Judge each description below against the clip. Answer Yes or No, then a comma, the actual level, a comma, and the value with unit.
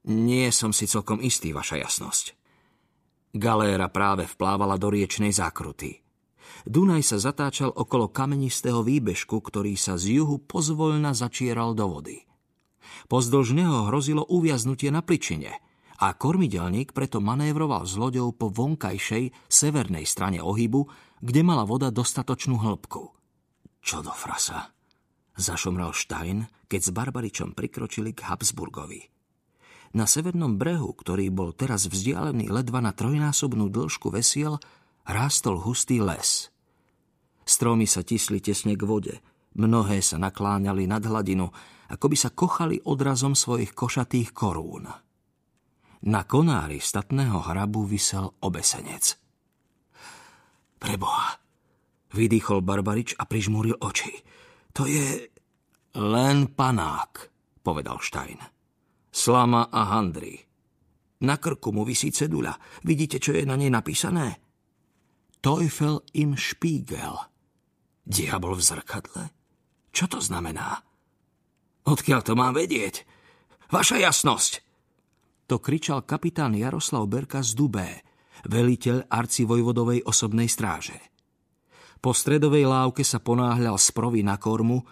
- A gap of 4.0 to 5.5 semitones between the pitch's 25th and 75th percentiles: Yes, average, 4.9 semitones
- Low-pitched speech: Yes, low, 120 Hz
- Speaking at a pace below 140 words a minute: Yes, slow, 110 wpm